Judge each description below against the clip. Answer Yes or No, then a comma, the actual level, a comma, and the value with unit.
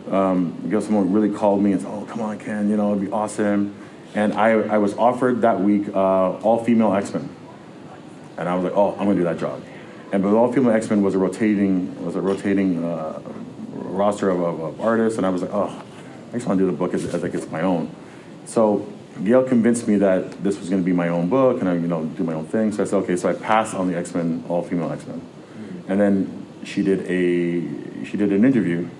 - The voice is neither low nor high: No, low, 100 Hz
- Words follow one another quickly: Yes, fast, 240 wpm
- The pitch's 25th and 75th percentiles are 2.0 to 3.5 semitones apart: Yes, average, 2.7 semitones